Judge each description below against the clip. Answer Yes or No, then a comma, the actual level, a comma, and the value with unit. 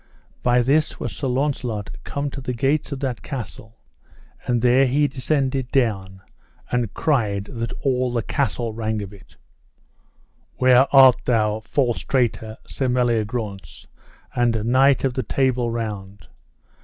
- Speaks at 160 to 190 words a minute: No, average, 140 wpm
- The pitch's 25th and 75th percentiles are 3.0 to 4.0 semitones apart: Yes, average, 3.3 semitones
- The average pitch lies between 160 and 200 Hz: No, low, 125 Hz